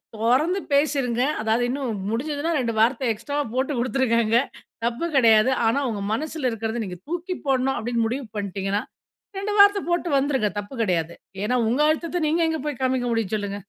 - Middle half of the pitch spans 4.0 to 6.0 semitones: Yes, average, 4.7 semitones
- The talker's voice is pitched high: Yes, very high, 250 Hz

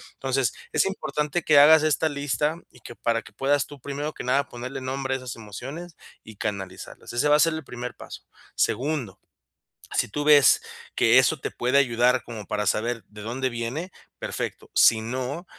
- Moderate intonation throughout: Yes, average, 4.0 semitones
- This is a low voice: Yes, low, 130 Hz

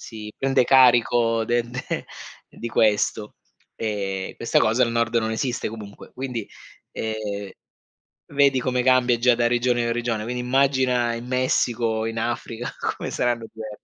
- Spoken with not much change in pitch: Yes, narrow, 1.9 semitones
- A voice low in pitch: Yes, low, 120 Hz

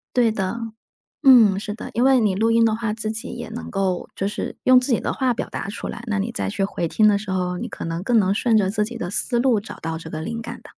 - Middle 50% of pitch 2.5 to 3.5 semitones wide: Yes, average, 3.2 semitones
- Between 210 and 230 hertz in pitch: Yes, high, 215 Hz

